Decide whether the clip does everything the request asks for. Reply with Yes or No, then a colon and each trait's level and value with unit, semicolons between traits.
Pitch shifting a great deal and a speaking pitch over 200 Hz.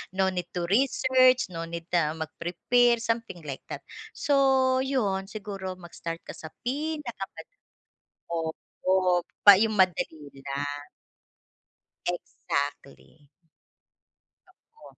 No: wide, 6.7 semitones; high, 190 Hz